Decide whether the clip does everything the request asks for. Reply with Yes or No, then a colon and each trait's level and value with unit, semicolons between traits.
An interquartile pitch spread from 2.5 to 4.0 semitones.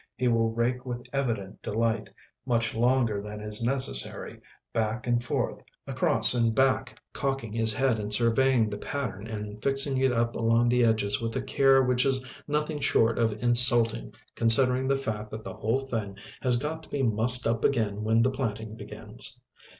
Yes: average, 2.9 semitones